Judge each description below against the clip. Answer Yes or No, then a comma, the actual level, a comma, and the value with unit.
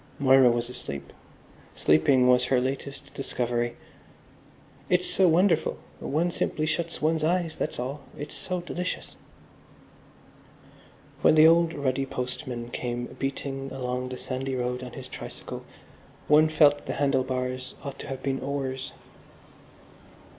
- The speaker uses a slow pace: Yes, slow, 130 wpm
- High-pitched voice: No, low, 135 Hz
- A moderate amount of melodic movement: Yes, average, 3.4 semitones